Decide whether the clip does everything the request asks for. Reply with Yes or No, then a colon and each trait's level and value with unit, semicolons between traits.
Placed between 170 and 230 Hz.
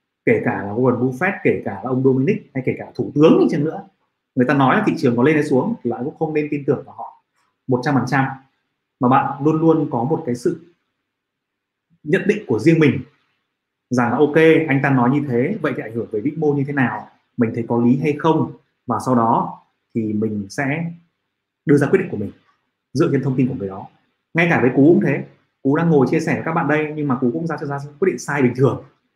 No: low, 135 Hz